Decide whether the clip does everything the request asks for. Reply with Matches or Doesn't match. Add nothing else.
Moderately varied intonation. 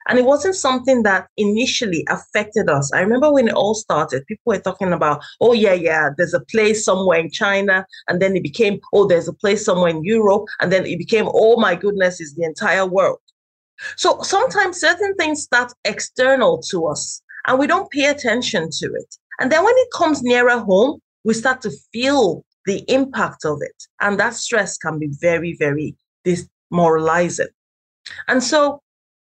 Doesn't match